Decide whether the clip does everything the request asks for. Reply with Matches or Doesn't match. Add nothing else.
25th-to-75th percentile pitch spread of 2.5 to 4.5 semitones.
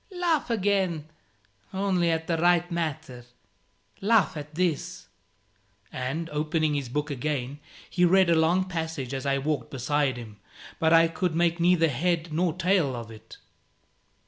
Matches